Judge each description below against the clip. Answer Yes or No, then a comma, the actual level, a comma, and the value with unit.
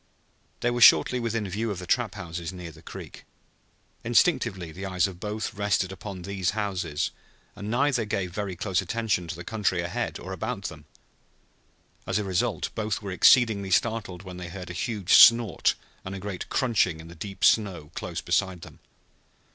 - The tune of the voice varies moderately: Yes, average, 3.4 semitones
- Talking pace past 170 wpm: Yes, average, 180 wpm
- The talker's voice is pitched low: Yes, very low, 95 Hz